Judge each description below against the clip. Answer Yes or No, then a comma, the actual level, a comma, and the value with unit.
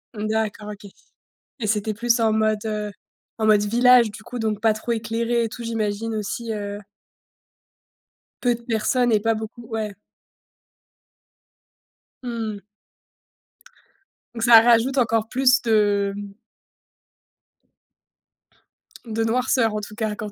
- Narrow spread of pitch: Yes, narrow, 1.7 semitones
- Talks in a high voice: Yes, high, 220 Hz